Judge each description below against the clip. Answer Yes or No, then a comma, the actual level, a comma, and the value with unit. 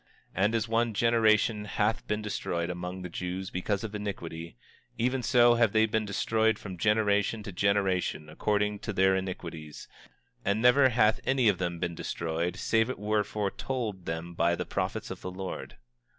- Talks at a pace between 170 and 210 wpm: Yes, average, 175 wpm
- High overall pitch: No, low, 105 Hz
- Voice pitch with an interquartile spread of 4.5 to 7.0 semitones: No, average, 3.6 semitones